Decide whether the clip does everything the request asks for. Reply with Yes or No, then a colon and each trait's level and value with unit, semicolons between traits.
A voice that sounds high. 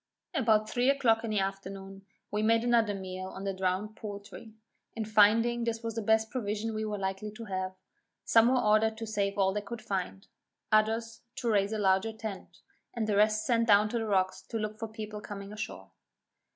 Yes: high, 215 Hz